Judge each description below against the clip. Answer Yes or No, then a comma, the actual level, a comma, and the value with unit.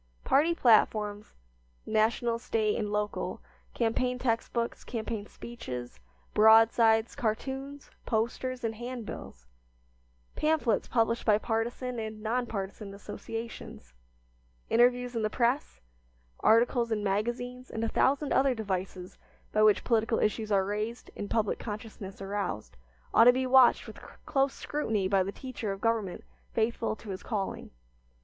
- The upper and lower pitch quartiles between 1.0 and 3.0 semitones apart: Yes, average, 2.7 semitones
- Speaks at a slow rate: Yes, slow, 130 wpm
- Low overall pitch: No, high, 225 Hz